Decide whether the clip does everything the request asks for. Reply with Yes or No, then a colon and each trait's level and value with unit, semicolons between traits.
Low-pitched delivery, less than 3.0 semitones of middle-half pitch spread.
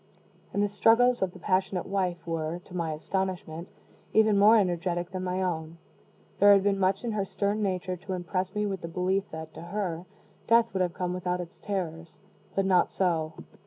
No: medium, 185 Hz; narrow, 2.4 semitones